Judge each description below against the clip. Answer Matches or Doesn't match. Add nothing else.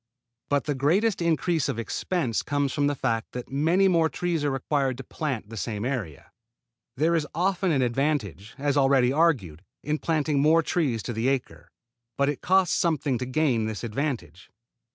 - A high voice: Doesn't match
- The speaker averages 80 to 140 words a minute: Doesn't match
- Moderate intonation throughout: Matches